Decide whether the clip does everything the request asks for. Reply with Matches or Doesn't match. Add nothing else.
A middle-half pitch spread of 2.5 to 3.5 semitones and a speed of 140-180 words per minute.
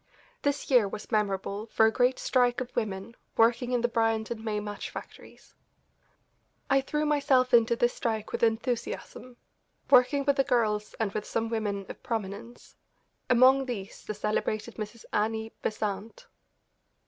Matches